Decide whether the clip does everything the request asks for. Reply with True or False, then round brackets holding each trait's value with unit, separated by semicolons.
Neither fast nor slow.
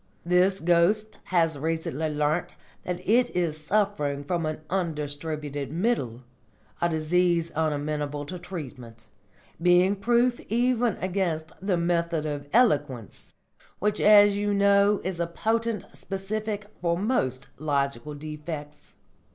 False (120 wpm)